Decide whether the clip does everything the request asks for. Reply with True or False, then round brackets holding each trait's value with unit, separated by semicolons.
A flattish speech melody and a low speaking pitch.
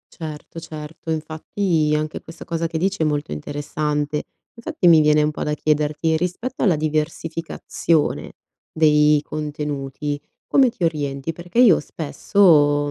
False (1.9 semitones; 155 Hz)